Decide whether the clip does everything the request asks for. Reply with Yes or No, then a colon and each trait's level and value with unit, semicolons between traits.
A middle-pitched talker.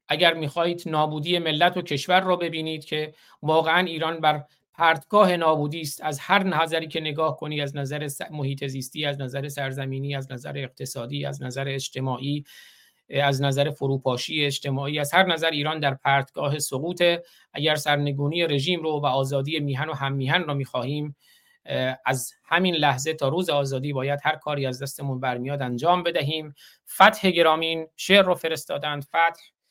Yes: medium, 150 Hz